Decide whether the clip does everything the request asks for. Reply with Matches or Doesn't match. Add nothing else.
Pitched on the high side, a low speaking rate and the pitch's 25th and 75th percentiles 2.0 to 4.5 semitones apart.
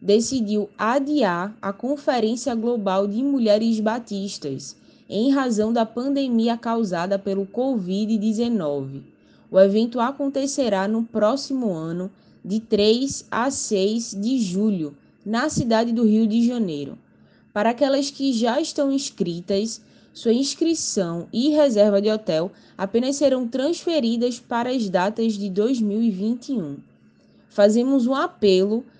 Matches